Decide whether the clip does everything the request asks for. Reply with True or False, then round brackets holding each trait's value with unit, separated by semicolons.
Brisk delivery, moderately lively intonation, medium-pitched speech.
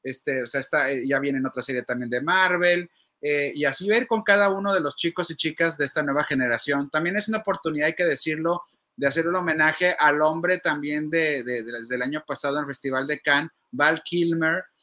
True (225 wpm; 3.7 semitones; 150 Hz)